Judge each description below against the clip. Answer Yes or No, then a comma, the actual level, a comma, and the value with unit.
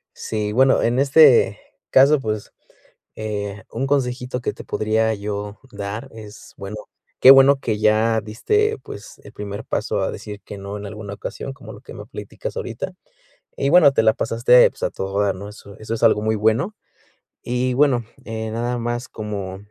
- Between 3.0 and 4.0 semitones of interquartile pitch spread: Yes, average, 3.3 semitones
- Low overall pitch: Yes, low, 110 Hz